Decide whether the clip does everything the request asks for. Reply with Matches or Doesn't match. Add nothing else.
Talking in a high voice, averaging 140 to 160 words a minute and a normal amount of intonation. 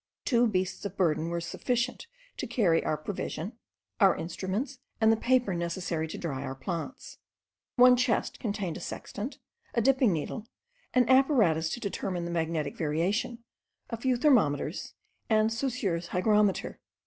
Doesn't match